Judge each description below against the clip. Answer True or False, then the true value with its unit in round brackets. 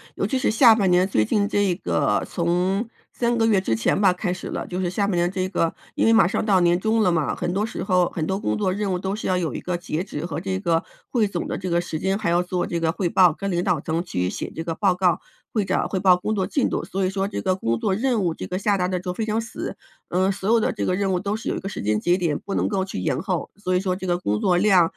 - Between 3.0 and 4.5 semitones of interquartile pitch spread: False (2.5 semitones)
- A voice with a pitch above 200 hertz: False (185 Hz)